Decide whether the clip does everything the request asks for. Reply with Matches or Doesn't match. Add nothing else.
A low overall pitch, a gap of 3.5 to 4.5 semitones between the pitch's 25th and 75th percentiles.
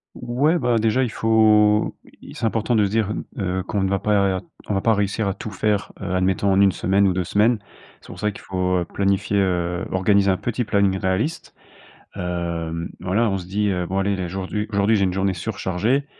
Doesn't match